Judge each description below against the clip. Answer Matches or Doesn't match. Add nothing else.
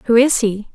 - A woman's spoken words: Matches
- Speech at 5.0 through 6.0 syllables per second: Doesn't match